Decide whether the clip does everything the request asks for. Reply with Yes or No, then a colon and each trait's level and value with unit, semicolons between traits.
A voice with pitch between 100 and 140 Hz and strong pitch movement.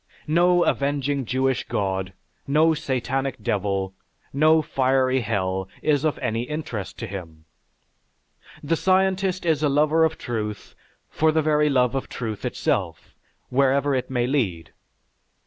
Yes: low, 135 Hz; wide, 5.7 semitones